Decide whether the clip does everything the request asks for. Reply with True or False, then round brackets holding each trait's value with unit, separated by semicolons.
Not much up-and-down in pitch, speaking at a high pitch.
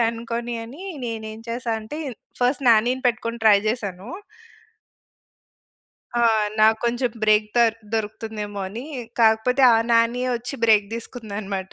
True (1.9 semitones; 230 Hz)